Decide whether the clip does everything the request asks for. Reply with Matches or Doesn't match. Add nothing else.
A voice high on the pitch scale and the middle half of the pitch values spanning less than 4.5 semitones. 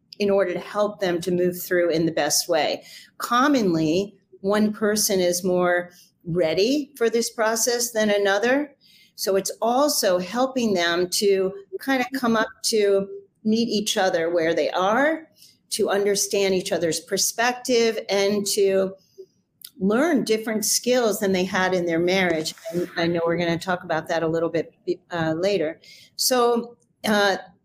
Matches